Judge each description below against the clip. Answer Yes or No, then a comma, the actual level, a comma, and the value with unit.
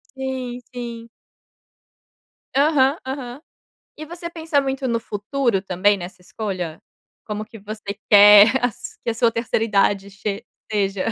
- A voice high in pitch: Yes, high, 225 Hz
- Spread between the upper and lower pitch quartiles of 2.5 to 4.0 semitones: No, average, 4.6 semitones